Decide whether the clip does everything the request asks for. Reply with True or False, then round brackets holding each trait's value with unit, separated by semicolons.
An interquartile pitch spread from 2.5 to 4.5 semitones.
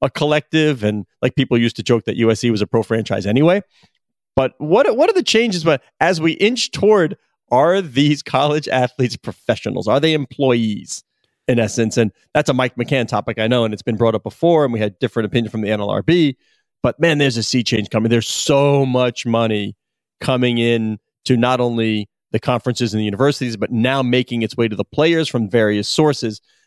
True (4.2 semitones)